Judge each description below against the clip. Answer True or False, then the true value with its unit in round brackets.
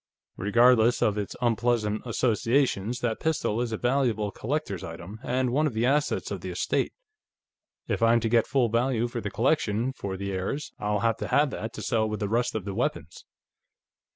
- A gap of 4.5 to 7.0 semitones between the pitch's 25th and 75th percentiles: False (3.0 semitones)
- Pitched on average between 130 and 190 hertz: False (115 Hz)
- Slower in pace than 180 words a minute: False (190 wpm)